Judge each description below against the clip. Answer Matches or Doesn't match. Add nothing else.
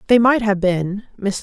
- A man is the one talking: Doesn't match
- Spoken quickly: Doesn't match